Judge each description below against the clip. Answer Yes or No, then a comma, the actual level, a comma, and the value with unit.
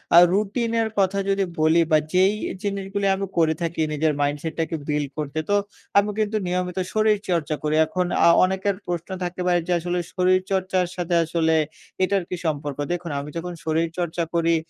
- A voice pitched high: No, medium, 180 Hz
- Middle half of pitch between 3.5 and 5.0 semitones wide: No, average, 3.1 semitones